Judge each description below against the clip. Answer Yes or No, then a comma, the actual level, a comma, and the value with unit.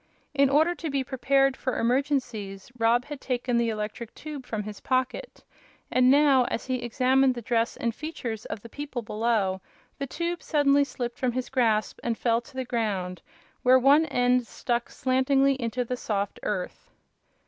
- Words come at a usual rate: Yes, average, 170 wpm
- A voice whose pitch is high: Yes, very high, 250 Hz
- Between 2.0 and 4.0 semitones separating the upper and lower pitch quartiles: Yes, average, 3.0 semitones